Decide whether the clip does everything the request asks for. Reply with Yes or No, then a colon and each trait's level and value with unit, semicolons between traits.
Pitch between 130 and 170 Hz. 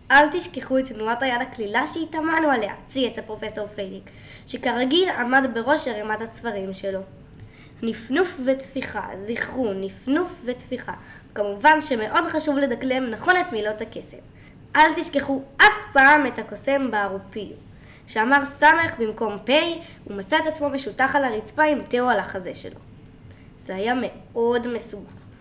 No: very high, 255 Hz